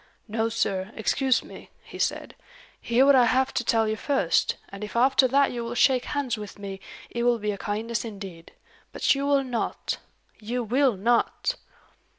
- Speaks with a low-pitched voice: No, high, 235 Hz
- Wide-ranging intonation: No, average, 3.6 semitones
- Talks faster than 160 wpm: Yes, average, 180 wpm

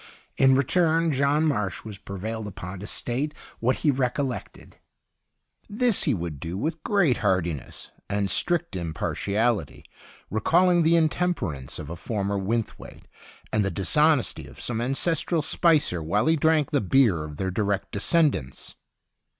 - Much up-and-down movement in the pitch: Yes, wide, 8.2 semitones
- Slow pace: No, average, 145 wpm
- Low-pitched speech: Yes, low, 120 Hz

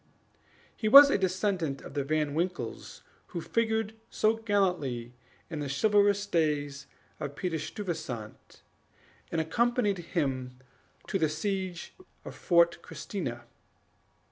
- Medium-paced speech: No, slow, 115 wpm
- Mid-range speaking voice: Yes, medium, 175 Hz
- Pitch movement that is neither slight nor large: No, wide, 5.9 semitones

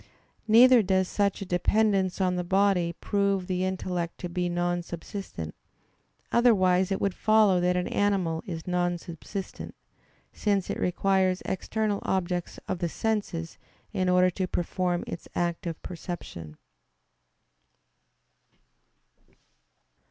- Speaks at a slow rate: Yes, slow, 120 wpm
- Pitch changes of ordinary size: No, narrow, 2.0 semitones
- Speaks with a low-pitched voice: No, medium, 185 Hz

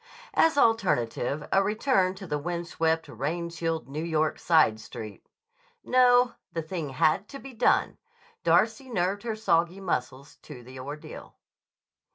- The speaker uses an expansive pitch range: Yes, wide, 5.9 semitones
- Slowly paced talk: No, average, 145 wpm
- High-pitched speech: No, medium, 170 Hz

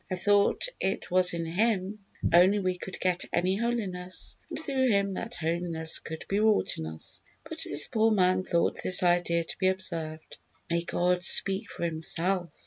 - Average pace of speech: Yes, average, 175 wpm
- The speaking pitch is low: No, medium, 185 Hz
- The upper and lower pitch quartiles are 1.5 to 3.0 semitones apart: Yes, average, 2.7 semitones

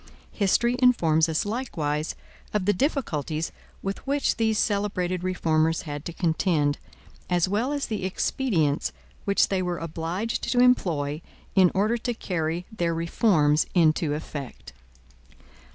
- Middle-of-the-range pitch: Yes, medium, 180 Hz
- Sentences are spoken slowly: Yes, slow, 130 wpm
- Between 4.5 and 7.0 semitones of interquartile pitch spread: Yes, average, 5.2 semitones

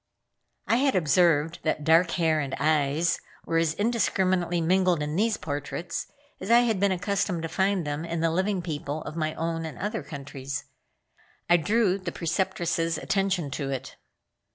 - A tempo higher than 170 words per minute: No, average, 165 wpm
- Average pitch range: Yes, average, 3.4 semitones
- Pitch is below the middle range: No, medium, 170 Hz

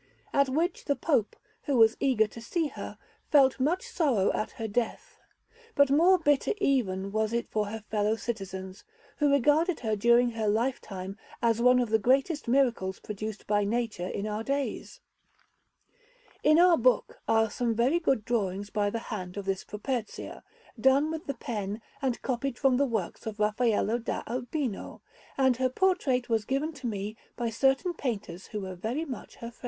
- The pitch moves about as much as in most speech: Yes, average, 4.6 semitones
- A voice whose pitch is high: Yes, high, 235 Hz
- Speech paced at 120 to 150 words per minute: No, average, 175 wpm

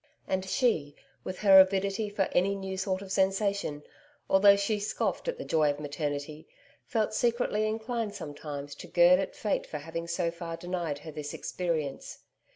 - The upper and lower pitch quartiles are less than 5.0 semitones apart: Yes, average, 4.3 semitones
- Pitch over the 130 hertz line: Yes, medium, 185 Hz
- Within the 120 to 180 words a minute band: Yes, average, 165 wpm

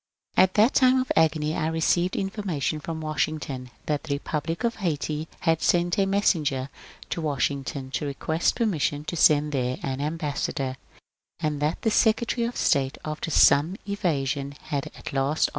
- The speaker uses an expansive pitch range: No, average, 3.8 semitones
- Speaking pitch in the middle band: Yes, medium, 155 Hz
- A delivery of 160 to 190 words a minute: Yes, average, 165 wpm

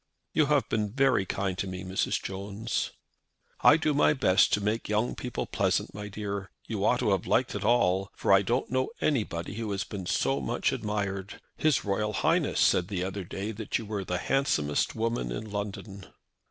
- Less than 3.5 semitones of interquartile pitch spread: Yes, average, 2.9 semitones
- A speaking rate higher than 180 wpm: Yes, average, 195 wpm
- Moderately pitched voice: No, low, 105 Hz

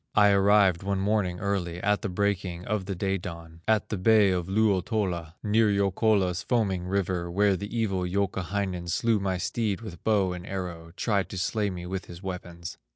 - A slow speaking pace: No, average, 180 wpm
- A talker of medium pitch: No, very low, 95 Hz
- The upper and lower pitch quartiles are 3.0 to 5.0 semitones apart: No, narrow, 2.4 semitones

